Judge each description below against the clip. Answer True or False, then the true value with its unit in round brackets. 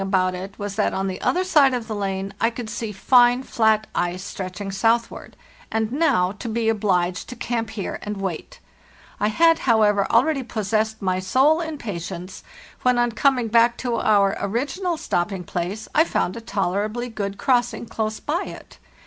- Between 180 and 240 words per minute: True (185 wpm)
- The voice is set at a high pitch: True (220 Hz)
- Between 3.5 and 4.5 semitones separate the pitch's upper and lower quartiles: True (3.8 semitones)